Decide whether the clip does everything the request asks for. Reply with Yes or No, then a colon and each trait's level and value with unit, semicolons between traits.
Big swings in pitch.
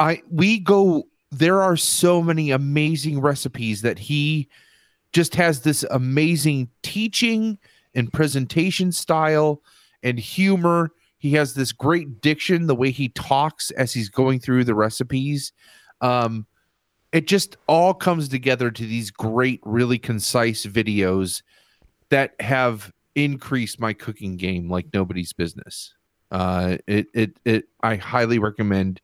Yes: wide, 5.8 semitones